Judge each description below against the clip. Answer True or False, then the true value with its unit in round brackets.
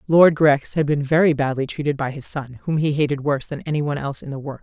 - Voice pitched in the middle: True (145 Hz)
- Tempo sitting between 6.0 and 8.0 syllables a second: True (6.5 syllables/s)